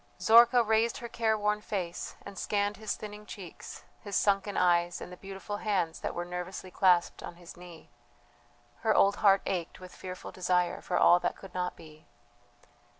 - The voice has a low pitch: No, high, 195 Hz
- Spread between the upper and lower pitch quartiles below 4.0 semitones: Yes, average, 2.8 semitones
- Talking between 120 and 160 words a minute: No, average, 170 wpm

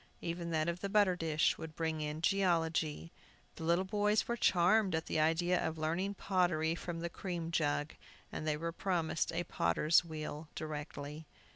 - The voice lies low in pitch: No, medium, 165 Hz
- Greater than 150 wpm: Yes, average, 170 wpm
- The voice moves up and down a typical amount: No, narrow, 2.3 semitones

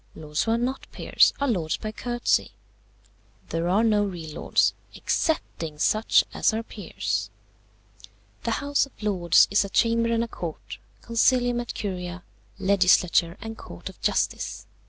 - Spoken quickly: No, average, 150 wpm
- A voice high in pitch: Yes, high, 205 Hz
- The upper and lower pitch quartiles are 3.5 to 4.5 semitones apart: No, average, 5.2 semitones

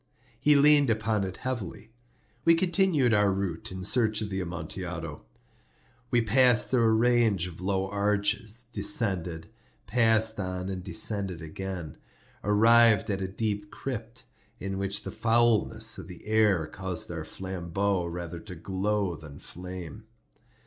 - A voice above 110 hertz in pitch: No, low, 100 Hz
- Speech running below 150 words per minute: Yes, average, 140 wpm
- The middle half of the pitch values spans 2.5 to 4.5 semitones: Yes, average, 3.5 semitones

